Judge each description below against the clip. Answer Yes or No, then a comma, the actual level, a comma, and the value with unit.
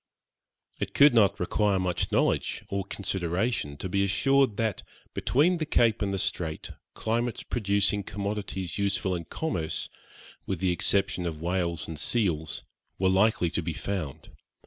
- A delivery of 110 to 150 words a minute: Yes, average, 145 wpm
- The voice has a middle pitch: No, low, 100 Hz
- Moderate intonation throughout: Yes, average, 3.6 semitones